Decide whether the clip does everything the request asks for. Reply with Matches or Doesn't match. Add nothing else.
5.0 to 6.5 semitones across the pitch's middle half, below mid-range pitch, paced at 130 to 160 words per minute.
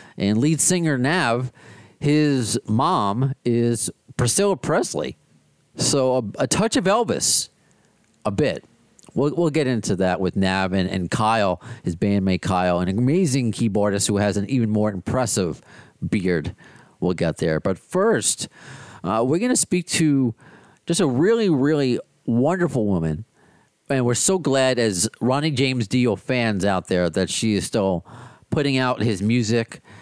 Matches